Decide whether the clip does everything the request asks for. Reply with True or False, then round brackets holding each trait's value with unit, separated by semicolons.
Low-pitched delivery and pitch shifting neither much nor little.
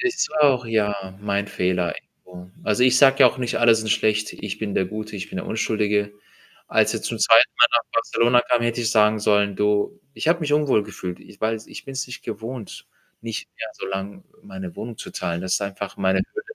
True (110 Hz; 3.1 semitones)